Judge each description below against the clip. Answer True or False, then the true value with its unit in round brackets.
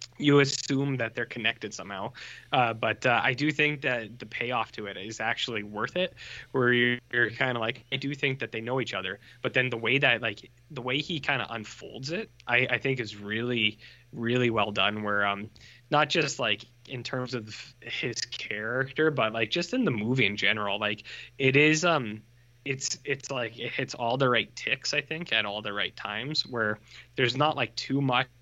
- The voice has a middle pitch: False (120 Hz)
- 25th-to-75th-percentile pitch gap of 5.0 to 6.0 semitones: False (3.5 semitones)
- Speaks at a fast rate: True (210 wpm)